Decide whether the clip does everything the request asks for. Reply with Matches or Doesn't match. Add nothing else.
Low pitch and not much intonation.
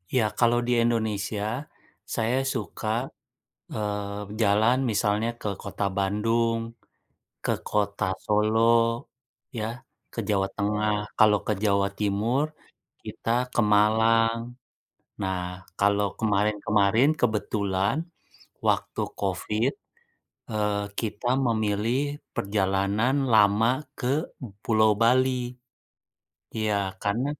Matches